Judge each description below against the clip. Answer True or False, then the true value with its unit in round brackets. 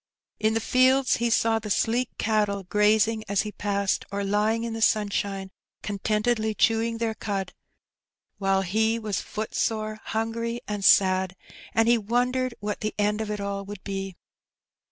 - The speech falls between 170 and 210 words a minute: False (160 wpm)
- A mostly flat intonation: True (2.0 semitones)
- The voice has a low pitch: False (215 Hz)